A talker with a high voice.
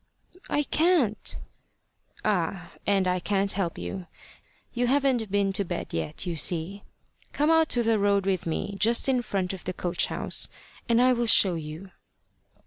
Yes: high, 200 Hz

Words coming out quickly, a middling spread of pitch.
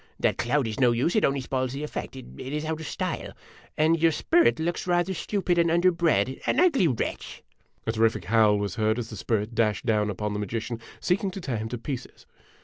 No: fast, 220 wpm; wide, 7.0 semitones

